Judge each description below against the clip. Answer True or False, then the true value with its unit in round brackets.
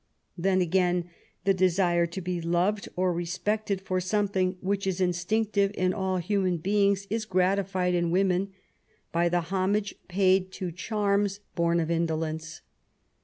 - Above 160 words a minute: True (170 wpm)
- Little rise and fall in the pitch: True (2.2 semitones)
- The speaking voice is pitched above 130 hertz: True (185 Hz)